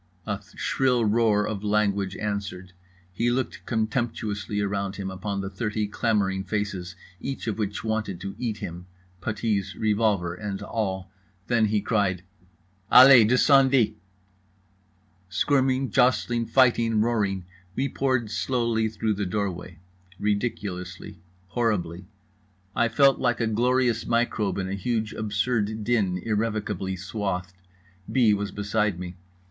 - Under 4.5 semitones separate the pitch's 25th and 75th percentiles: Yes, average, 3.2 semitones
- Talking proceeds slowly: Yes, slow, 120 wpm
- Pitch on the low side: Yes, low, 105 Hz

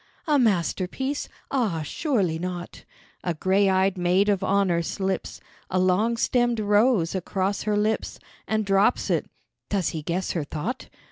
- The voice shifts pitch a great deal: No, average, 3.3 semitones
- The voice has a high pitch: Yes, high, 195 Hz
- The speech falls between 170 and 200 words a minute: No, average, 145 wpm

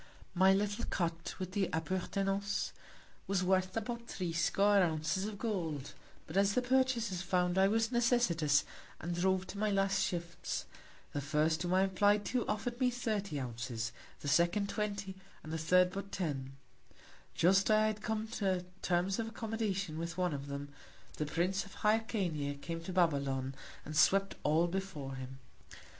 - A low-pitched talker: No, medium, 185 Hz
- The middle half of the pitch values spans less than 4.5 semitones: Yes, average, 4.1 semitones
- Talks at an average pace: Yes, average, 160 wpm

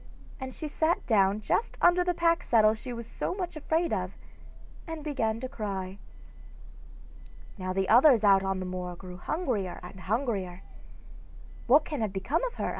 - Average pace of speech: Yes, average, 170 wpm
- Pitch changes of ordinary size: No, wide, 8.2 semitones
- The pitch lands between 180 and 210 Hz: No, high, 225 Hz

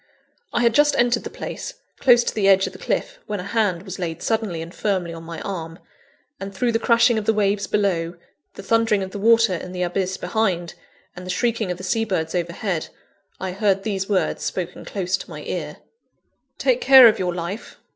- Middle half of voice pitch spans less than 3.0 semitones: No, average, 3.9 semitones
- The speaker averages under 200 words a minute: No, fast, 205 wpm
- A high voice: Yes, high, 195 Hz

